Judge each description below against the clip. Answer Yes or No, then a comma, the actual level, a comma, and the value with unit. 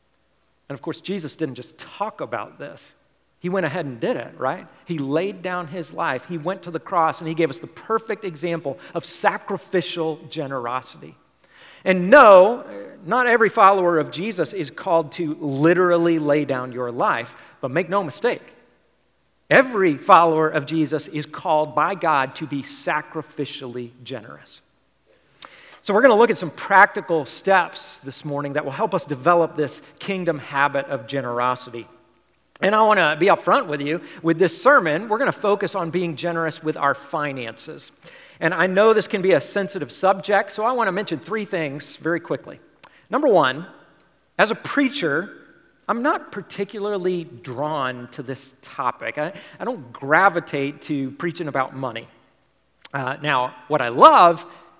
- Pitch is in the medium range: Yes, medium, 165 Hz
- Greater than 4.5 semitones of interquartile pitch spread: Yes, average, 5.1 semitones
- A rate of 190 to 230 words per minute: No, average, 165 wpm